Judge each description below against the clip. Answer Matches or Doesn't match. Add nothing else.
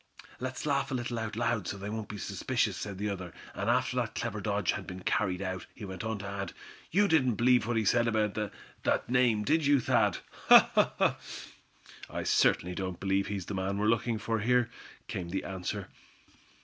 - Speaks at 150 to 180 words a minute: Doesn't match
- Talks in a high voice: Doesn't match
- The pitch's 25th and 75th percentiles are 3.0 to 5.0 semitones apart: Matches